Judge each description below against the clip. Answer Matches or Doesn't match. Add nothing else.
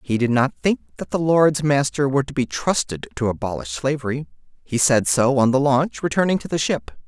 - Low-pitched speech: Matches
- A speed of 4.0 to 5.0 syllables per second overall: Doesn't match